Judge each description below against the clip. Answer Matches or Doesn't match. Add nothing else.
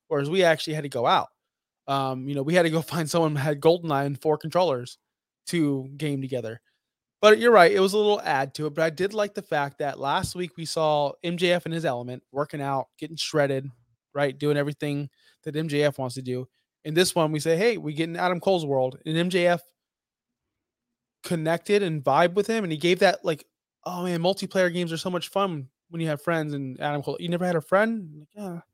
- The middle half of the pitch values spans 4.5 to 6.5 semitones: Doesn't match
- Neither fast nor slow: Doesn't match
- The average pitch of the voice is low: Doesn't match